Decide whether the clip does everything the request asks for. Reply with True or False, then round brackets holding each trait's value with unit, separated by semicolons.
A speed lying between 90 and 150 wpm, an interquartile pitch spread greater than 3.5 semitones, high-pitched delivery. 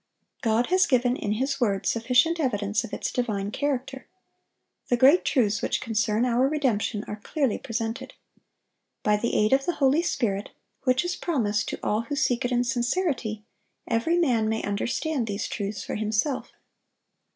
False (165 wpm; 4.1 semitones; 240 Hz)